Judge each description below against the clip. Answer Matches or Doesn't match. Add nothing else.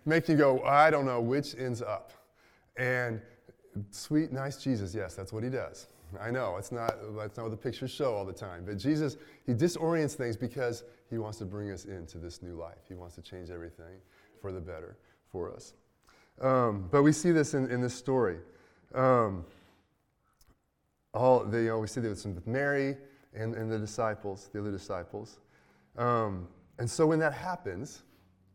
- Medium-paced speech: Matches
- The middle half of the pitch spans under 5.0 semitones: Doesn't match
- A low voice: Matches